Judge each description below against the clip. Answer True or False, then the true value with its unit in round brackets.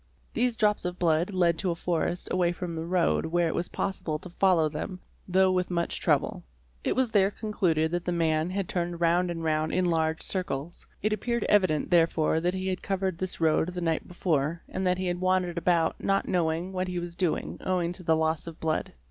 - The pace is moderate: False (220 wpm)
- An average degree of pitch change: False (2.2 semitones)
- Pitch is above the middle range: False (175 Hz)